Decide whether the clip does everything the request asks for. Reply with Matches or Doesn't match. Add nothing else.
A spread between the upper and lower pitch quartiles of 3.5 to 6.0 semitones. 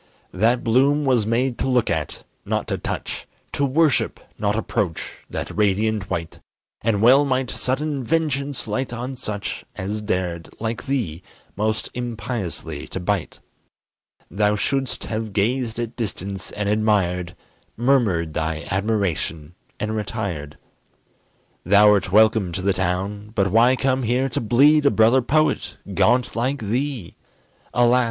Matches